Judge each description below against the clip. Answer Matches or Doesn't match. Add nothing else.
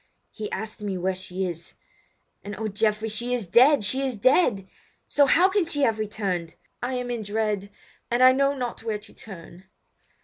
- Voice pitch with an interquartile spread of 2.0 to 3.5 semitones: Doesn't match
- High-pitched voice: Matches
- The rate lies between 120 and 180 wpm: Doesn't match